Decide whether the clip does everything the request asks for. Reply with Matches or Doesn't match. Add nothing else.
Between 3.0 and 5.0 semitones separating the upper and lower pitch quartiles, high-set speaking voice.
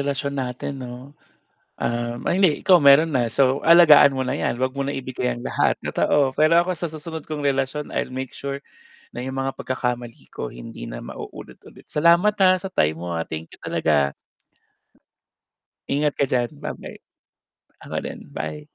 Doesn't match